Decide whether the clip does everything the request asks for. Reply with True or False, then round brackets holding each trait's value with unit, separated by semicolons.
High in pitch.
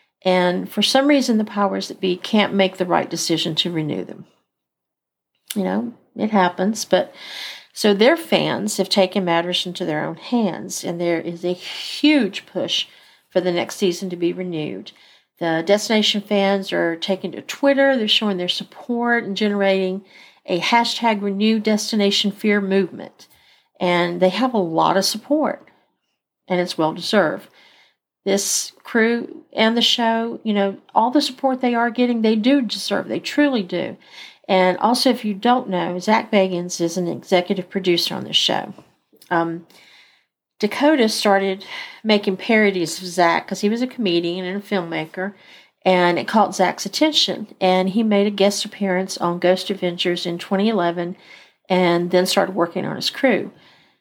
True (195 Hz)